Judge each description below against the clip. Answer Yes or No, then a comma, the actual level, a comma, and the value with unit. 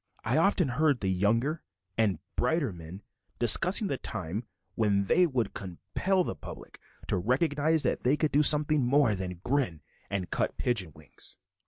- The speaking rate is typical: Yes, average, 160 wpm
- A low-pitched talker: Yes, low, 125 Hz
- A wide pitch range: Yes, wide, 7.6 semitones